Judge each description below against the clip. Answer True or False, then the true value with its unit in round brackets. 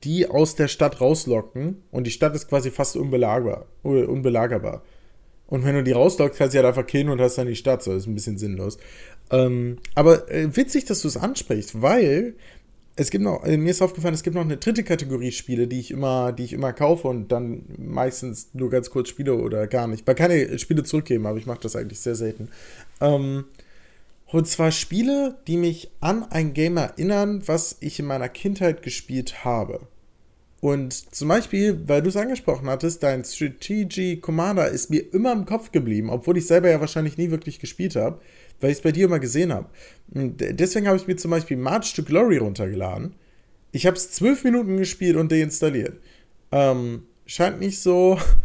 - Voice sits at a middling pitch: True (150 Hz)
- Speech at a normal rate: False (195 wpm)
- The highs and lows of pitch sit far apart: True (5.7 semitones)